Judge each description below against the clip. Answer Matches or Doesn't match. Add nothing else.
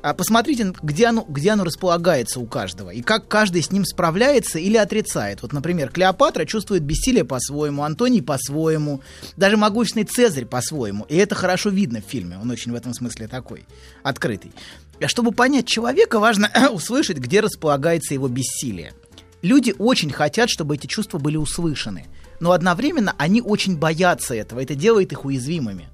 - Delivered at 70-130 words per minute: Doesn't match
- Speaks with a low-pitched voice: Doesn't match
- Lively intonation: Matches